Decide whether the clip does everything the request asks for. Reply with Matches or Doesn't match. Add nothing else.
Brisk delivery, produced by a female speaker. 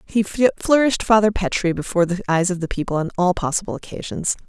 Doesn't match